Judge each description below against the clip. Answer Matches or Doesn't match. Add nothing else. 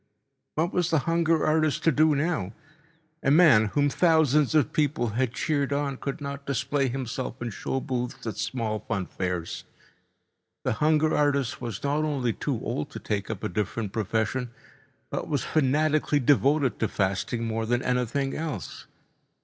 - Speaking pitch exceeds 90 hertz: Matches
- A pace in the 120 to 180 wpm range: Matches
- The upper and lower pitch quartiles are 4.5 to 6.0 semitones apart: Matches